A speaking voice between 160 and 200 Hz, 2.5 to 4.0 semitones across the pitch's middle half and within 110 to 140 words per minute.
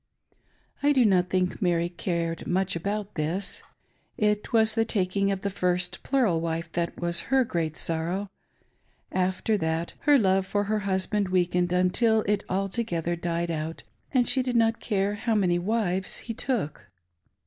No: high, 190 Hz; average, 3.7 semitones; average, 160 wpm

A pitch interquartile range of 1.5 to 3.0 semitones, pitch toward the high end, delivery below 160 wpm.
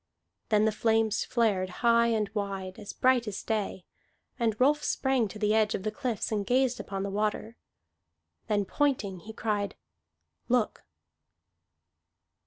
Yes: narrow, 2.5 semitones; high, 215 Hz; average, 145 wpm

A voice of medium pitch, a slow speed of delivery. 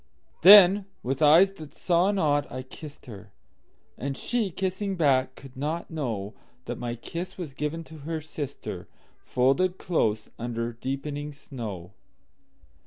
Yes: medium, 145 Hz; slow, 120 wpm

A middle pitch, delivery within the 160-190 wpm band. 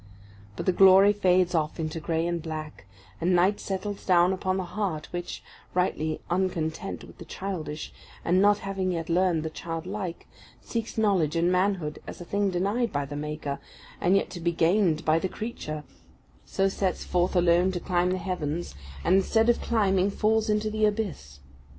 Yes: medium, 180 Hz; average, 175 wpm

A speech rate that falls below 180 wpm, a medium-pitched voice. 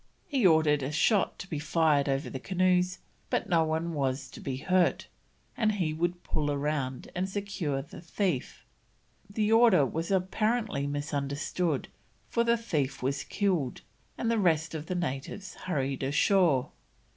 Yes: average, 155 wpm; medium, 160 Hz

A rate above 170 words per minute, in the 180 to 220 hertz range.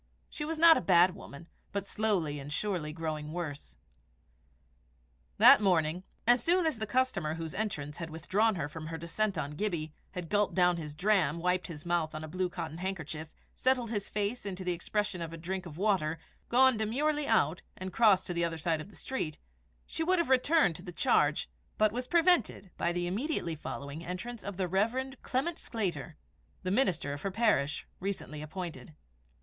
Yes: average, 190 wpm; medium, 185 Hz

